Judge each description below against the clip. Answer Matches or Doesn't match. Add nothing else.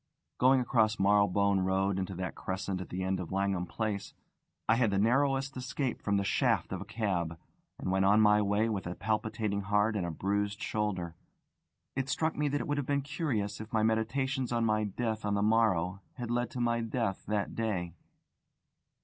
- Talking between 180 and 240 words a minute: Matches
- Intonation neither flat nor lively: Matches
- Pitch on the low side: Matches